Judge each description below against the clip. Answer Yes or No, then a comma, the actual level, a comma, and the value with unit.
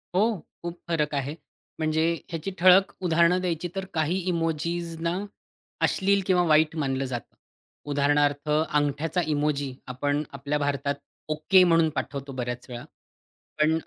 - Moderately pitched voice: Yes, medium, 155 Hz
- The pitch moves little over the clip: No, average, 3.0 semitones